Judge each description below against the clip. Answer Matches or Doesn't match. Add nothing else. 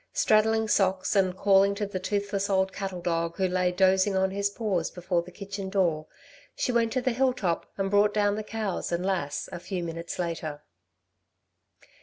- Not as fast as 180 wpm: Doesn't match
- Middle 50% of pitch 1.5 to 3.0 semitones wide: Matches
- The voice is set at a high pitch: Matches